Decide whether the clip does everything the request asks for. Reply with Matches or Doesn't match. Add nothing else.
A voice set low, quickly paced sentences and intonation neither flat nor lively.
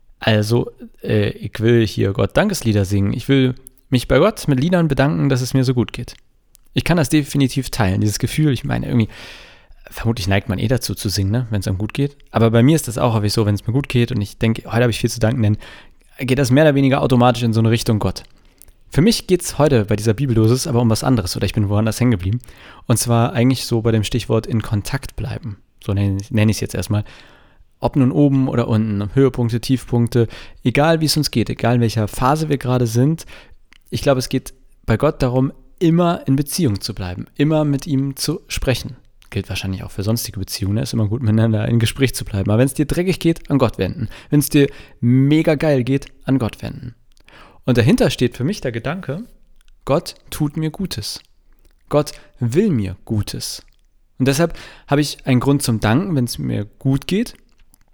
Matches